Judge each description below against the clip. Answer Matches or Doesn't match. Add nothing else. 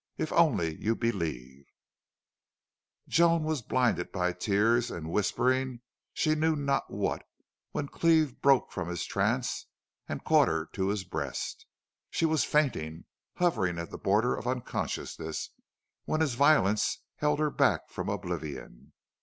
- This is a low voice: Matches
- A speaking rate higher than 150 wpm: Doesn't match